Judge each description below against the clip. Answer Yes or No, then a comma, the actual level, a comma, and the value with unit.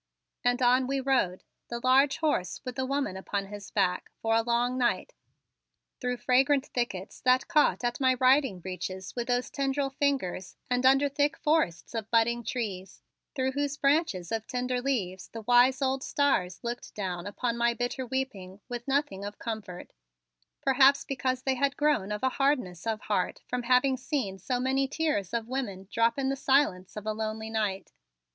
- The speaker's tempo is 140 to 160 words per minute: No, average, 175 wpm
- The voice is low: No, high, 245 Hz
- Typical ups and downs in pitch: Yes, average, 4.4 semitones